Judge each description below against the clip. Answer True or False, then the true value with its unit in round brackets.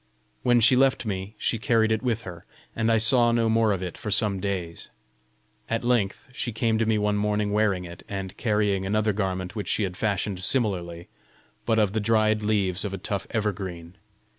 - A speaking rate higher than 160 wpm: True (195 wpm)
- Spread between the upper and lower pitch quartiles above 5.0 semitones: False (2.7 semitones)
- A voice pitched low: True (105 Hz)